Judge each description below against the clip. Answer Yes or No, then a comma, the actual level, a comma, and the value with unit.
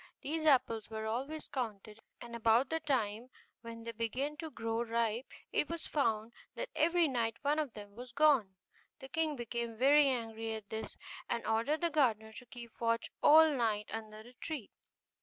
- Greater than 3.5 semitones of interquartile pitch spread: Yes, average, 4.6 semitones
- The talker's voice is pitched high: Yes, high, 235 Hz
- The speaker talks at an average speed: Yes, average, 175 wpm